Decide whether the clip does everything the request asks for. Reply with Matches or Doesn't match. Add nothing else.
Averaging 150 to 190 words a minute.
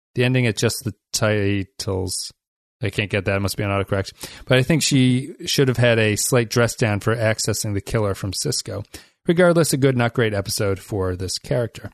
Doesn't match